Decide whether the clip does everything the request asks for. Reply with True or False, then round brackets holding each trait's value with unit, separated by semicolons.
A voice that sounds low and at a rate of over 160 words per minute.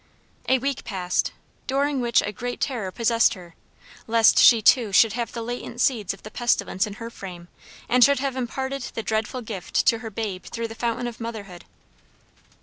False (230 Hz; 185 wpm)